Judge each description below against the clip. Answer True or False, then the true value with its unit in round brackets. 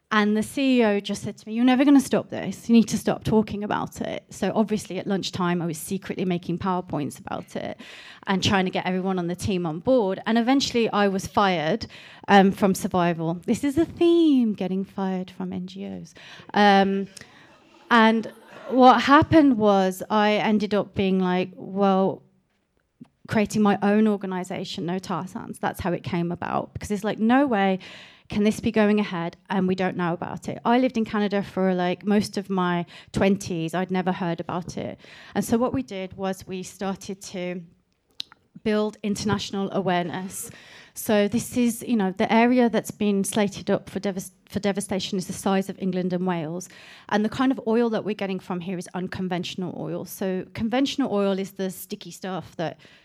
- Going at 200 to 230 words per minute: False (190 wpm)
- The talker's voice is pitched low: False (195 Hz)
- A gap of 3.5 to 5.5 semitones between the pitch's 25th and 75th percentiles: False (2.5 semitones)